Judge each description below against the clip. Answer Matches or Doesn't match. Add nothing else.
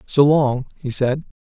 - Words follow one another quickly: Doesn't match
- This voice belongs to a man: Matches